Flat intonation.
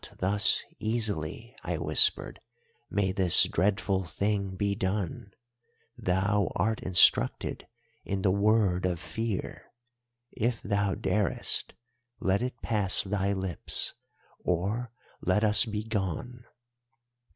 Yes: narrow, 2.3 semitones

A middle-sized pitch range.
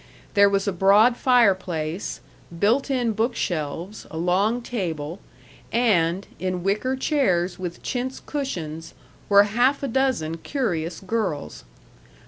No: wide, 5.9 semitones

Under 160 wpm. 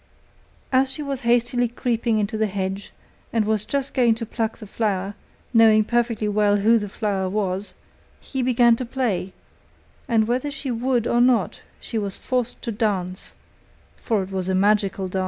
No: average, 175 wpm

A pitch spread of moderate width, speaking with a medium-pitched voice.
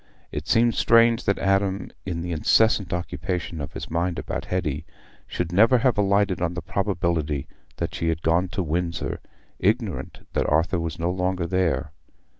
No: average, 3.0 semitones; very low, 90 Hz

